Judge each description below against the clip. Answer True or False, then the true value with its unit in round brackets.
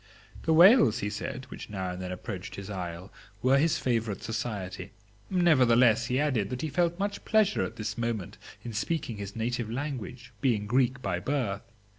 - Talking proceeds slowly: False (175 wpm)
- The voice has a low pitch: True (120 Hz)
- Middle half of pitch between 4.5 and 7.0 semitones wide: True (5.0 semitones)